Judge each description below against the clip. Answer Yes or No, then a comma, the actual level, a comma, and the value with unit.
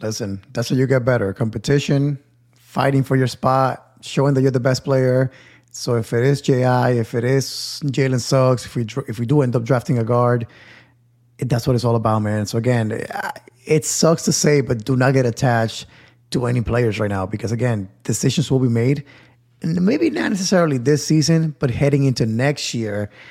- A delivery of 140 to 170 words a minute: No, average, 200 wpm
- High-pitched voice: No, low, 130 Hz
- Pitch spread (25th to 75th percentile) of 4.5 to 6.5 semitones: No, average, 2.9 semitones